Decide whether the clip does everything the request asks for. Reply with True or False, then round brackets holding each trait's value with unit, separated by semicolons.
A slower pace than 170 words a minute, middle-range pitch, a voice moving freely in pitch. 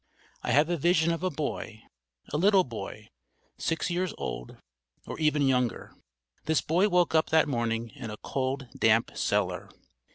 True (160 wpm; 145 Hz; 6.2 semitones)